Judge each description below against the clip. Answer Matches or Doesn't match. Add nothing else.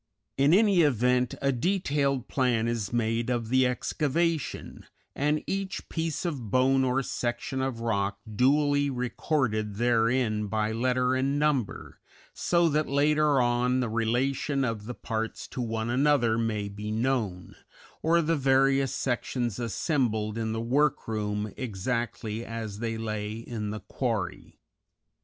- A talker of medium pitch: Doesn't match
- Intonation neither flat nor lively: Matches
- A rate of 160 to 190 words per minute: Doesn't match